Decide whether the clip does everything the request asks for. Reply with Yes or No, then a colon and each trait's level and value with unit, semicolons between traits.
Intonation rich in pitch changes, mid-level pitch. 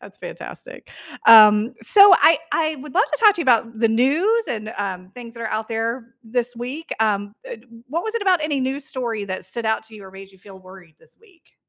No: wide, 6.4 semitones; high, 230 Hz